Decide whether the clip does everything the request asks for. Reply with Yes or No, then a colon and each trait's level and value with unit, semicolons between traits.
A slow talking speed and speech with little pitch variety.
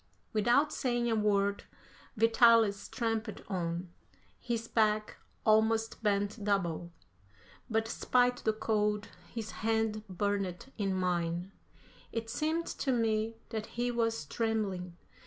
Yes: slow, 115 wpm; narrow, 2.3 semitones